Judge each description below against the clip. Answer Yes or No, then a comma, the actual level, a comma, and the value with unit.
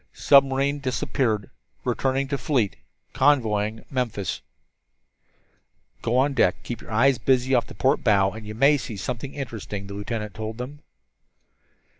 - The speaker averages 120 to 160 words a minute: Yes, average, 140 wpm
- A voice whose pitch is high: No, low, 125 Hz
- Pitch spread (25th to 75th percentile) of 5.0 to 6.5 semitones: No, average, 4.0 semitones